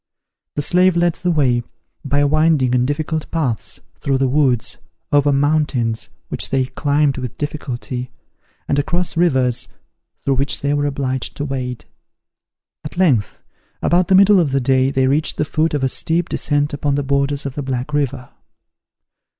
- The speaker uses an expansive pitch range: No, narrow, 2.6 semitones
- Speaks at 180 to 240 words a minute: No, average, 165 wpm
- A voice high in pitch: No, medium, 140 Hz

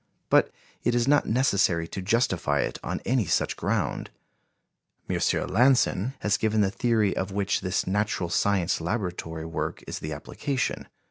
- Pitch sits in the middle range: No, low, 100 Hz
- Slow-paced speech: No, average, 150 wpm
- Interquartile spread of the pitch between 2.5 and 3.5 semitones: No, average, 4.9 semitones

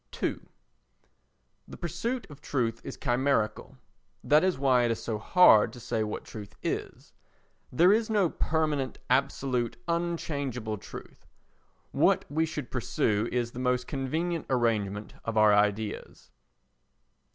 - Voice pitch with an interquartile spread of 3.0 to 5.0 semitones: No, wide, 5.6 semitones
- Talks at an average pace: No, slow, 130 wpm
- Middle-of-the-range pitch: No, low, 125 Hz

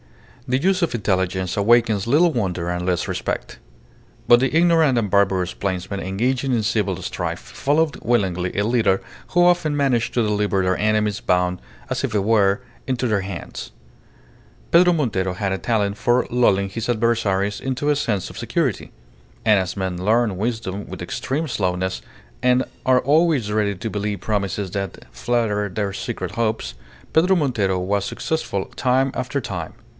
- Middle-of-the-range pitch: No, low, 110 Hz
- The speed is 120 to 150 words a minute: No, average, 160 wpm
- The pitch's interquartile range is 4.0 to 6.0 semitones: Yes, average, 4.6 semitones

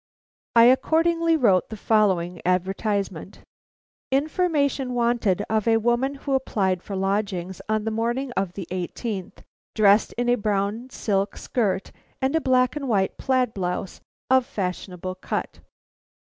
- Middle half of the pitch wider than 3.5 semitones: Yes, average, 5.0 semitones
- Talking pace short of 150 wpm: Yes, average, 140 wpm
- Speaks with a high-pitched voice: Yes, high, 220 Hz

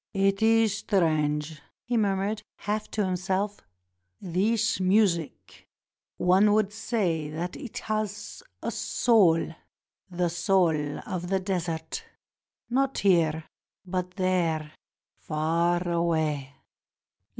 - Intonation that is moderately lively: Yes, average, 3.9 semitones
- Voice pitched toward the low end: No, medium, 185 Hz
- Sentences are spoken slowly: Yes, slow, 105 wpm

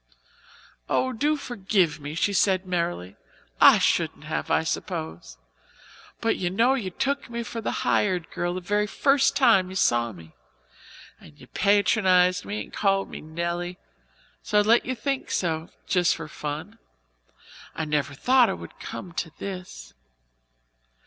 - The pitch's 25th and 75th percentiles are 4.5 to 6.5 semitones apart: Yes, average, 5.2 semitones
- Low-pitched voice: No, medium, 185 Hz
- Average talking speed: Yes, average, 155 wpm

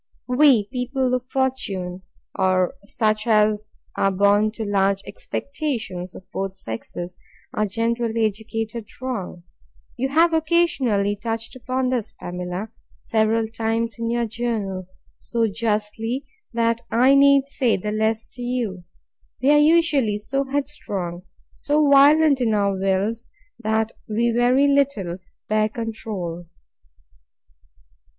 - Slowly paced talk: Yes, slow, 120 wpm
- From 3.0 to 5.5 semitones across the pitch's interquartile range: Yes, average, 4.0 semitones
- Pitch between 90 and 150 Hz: No, high, 225 Hz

